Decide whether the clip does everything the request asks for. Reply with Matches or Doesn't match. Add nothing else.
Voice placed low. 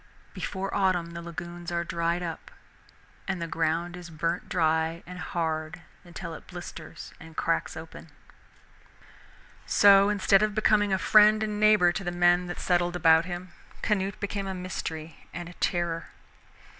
Doesn't match